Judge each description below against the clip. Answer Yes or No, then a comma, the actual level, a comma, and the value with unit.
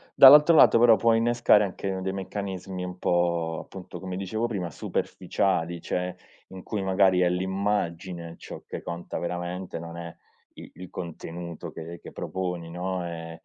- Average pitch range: No, narrow, 2.2 semitones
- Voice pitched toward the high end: No, very low, 90 Hz